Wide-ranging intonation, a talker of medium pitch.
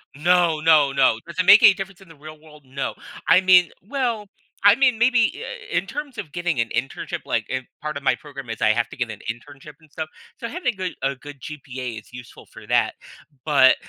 Yes: wide, 6.1 semitones; medium, 155 Hz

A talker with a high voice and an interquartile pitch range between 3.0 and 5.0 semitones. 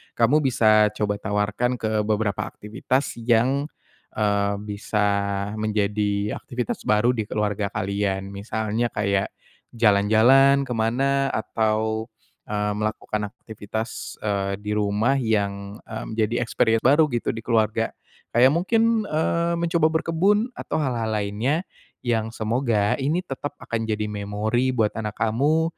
No: low, 110 Hz; average, 3.8 semitones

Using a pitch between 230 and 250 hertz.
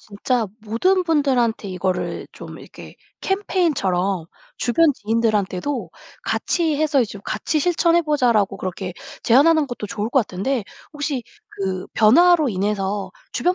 Yes: high, 235 Hz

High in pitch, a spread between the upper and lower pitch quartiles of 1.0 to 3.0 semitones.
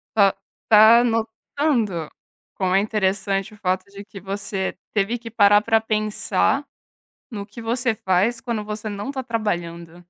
Yes: high, 210 Hz; narrow, 2.6 semitones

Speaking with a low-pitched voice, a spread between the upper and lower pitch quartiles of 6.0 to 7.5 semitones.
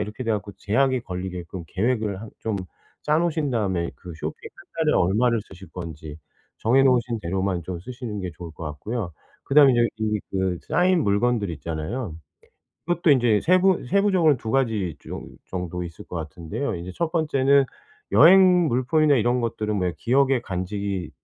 Yes: low, 110 Hz; wide, 6.7 semitones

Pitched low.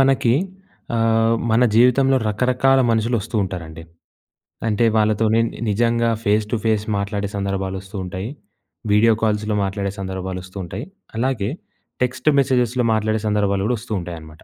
Yes: low, 110 Hz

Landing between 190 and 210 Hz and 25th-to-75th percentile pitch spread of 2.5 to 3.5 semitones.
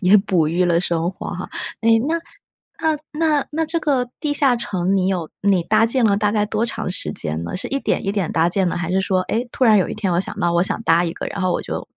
No: high, 195 Hz; average, 4.9 semitones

